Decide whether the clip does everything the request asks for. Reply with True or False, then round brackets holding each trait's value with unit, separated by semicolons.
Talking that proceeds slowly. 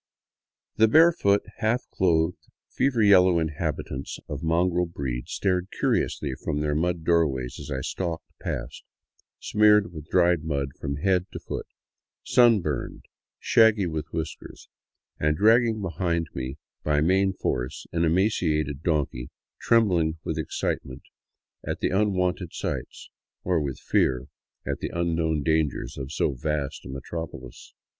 True (130 wpm)